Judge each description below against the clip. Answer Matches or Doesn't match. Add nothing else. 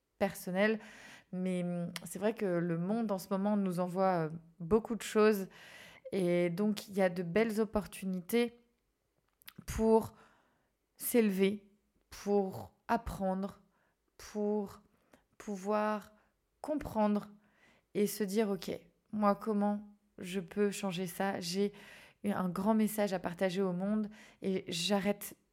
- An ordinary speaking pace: Doesn't match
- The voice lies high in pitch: Matches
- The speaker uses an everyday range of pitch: Doesn't match